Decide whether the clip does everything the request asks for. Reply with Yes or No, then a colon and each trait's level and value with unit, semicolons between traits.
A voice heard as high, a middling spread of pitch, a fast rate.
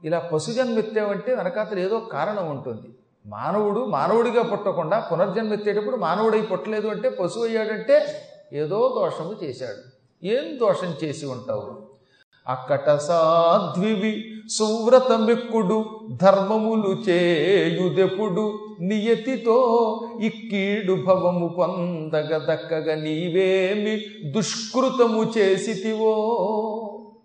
No: high, 215 Hz; average, 3.6 semitones; average, 80 wpm